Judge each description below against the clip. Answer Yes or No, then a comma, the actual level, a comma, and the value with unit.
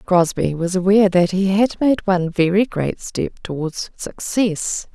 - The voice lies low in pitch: No, medium, 185 Hz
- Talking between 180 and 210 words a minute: No, average, 160 wpm